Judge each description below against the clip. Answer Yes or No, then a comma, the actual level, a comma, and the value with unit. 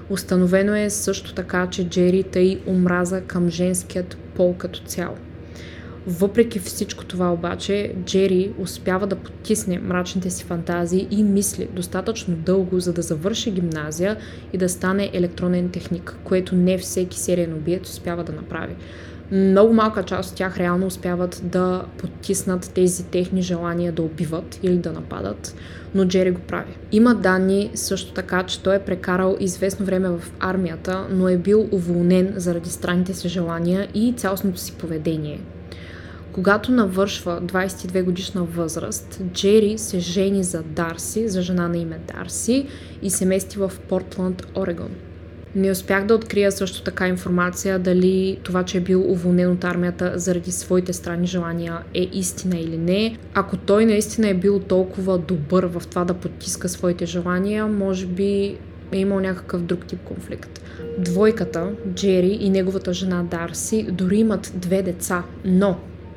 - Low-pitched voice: No, medium, 185 Hz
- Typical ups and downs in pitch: No, narrow, 1.6 semitones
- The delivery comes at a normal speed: Yes, average, 150 wpm